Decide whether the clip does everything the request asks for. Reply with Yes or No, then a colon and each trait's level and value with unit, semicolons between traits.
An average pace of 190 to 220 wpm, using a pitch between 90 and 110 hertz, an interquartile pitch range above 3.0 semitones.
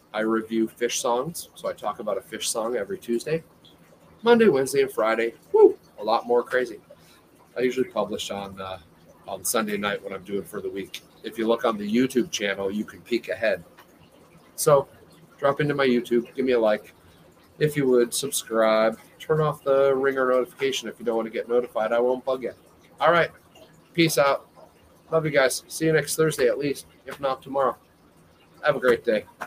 No: average, 195 wpm; low, 125 Hz; average, 4.1 semitones